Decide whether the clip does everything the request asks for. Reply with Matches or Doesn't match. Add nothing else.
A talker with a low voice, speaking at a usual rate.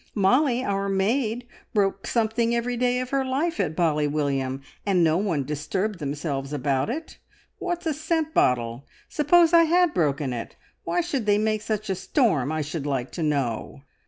Doesn't match